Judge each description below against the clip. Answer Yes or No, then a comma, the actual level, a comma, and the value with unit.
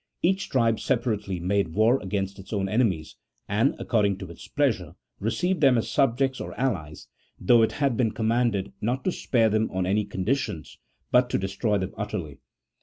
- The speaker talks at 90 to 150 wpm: No, average, 180 wpm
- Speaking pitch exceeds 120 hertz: No, low, 110 Hz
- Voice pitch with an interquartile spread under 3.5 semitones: No, average, 4.3 semitones